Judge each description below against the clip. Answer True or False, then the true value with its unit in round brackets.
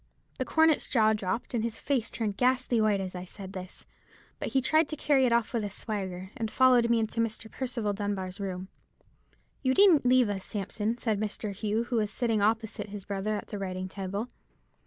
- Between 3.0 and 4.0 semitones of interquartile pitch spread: True (3.4 semitones)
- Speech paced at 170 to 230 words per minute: True (200 wpm)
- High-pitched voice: True (215 Hz)